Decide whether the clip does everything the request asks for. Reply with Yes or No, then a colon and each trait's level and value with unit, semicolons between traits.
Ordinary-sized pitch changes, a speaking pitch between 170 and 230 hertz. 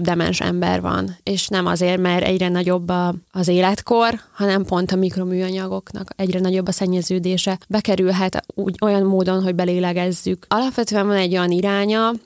No: narrow, 1.5 semitones; medium, 185 Hz